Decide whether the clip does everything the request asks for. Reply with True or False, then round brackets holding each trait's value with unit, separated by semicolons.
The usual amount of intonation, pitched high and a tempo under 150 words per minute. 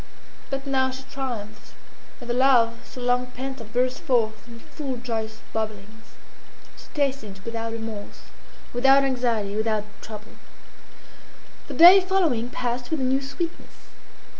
True (3.2 semitones; 245 Hz; 140 wpm)